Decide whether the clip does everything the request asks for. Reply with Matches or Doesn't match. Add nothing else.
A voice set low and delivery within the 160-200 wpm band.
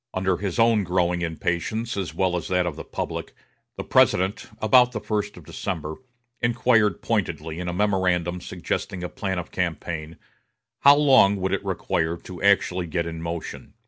Matches